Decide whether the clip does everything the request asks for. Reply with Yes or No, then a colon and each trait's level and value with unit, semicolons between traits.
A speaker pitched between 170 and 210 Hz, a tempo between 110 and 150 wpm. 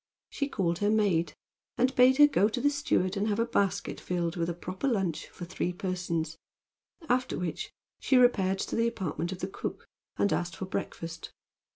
No: high, 190 Hz; average, 190 wpm